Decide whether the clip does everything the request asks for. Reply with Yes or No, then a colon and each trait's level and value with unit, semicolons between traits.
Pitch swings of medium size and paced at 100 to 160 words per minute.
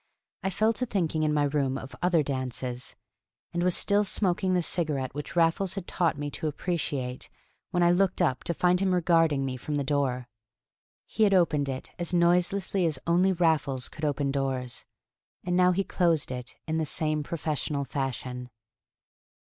No: average, 4.6 semitones; average, 175 wpm